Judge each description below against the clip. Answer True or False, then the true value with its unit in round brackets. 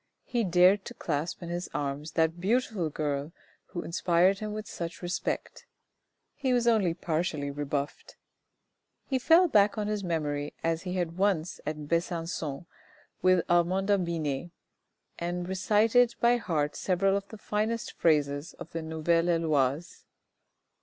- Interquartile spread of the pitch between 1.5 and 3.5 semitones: False (4.1 semitones)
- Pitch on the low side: False (175 Hz)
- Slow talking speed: False (145 wpm)